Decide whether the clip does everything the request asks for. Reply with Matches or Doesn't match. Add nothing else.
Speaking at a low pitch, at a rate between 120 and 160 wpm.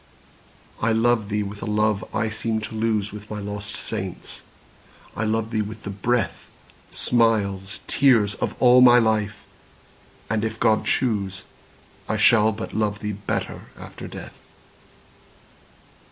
Matches